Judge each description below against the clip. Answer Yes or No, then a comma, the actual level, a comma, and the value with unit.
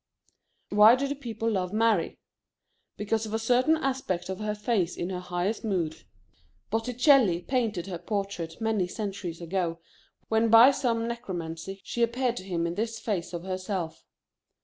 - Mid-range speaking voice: No, high, 210 Hz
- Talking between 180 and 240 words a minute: No, average, 155 wpm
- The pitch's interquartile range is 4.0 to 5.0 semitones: Yes, average, 4.3 semitones